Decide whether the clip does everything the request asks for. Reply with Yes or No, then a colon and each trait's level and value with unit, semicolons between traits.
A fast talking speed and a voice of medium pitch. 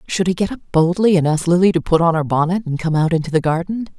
Yes: fast, 285 wpm; medium, 175 Hz